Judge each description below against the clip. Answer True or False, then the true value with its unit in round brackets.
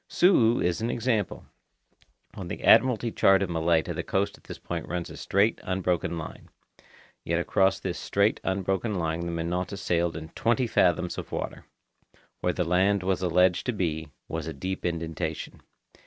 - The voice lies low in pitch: True (90 Hz)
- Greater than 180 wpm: False (170 wpm)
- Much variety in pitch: False (2.9 semitones)